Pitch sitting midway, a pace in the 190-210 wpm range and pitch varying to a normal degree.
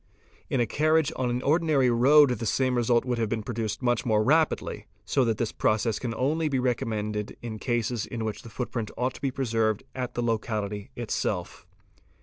No: low, 120 Hz; average, 195 wpm; average, 3.0 semitones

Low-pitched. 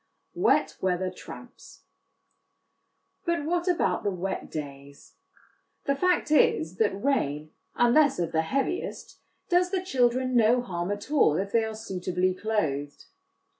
No: high, 210 Hz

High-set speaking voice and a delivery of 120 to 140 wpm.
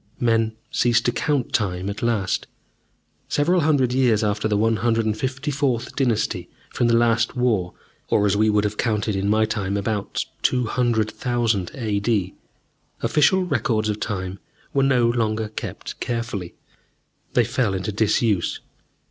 No: low, 110 Hz; slow, 135 wpm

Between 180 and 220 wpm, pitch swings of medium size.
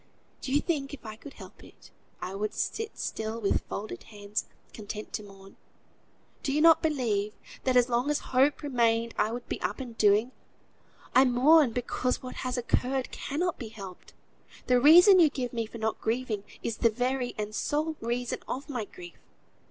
Yes: average, 185 wpm; average, 4.0 semitones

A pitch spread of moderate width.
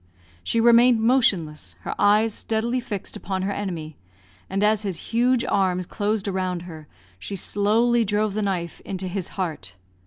Yes: average, 3.4 semitones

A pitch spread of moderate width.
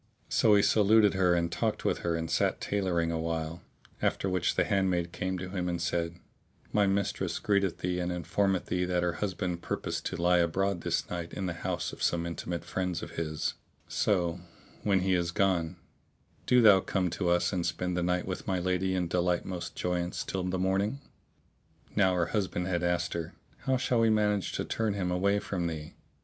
No: narrow, 2.0 semitones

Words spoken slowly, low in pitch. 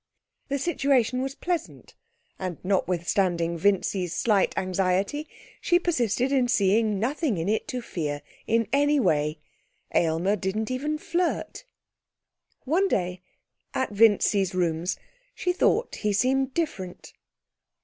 No: slow, 120 wpm; high, 210 Hz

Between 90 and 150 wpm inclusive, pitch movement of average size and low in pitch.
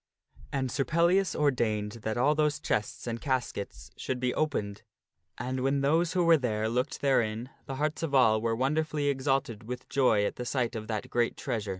No: average, 190 wpm; average, 4.1 semitones; low, 130 Hz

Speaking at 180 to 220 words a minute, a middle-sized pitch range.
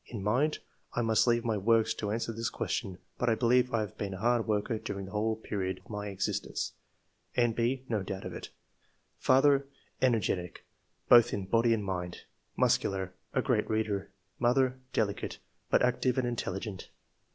Yes: average, 185 wpm; average, 3.2 semitones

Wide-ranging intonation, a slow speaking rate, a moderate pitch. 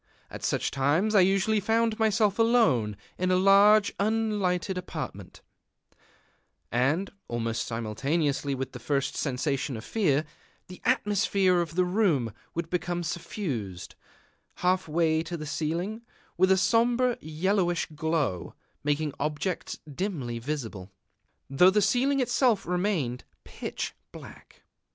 Yes: wide, 6.3 semitones; slow, 125 wpm; medium, 175 Hz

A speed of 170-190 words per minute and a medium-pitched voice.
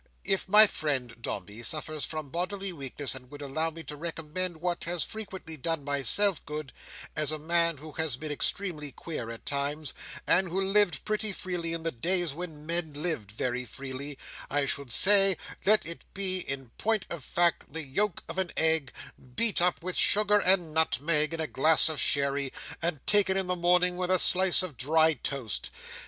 Yes: average, 185 wpm; medium, 160 Hz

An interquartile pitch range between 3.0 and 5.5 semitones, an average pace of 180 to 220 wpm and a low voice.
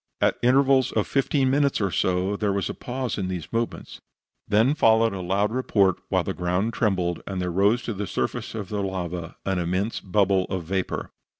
Yes: average, 3.7 semitones; average, 195 wpm; low, 100 Hz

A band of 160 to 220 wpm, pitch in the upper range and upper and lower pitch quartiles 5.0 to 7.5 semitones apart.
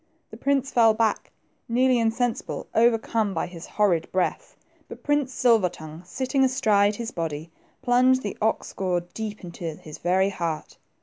No: average, 150 wpm; high, 215 Hz; wide, 5.6 semitones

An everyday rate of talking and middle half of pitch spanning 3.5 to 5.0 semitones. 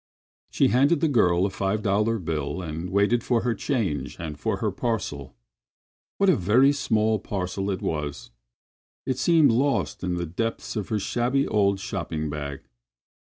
No: average, 165 wpm; wide, 5.6 semitones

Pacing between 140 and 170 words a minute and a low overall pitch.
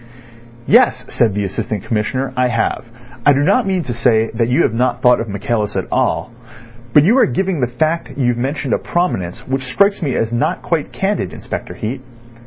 No: average, 195 wpm; low, 125 Hz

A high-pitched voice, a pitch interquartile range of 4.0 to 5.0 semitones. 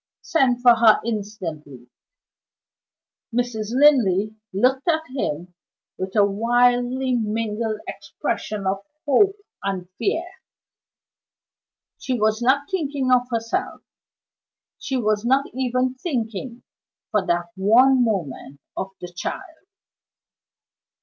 Yes: high, 235 Hz; average, 4.3 semitones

